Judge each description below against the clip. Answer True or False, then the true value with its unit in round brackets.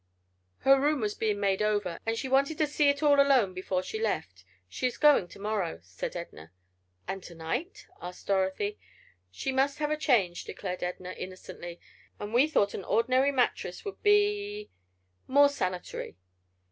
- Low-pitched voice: False (215 Hz)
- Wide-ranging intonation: True (7.5 semitones)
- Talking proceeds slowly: False (165 wpm)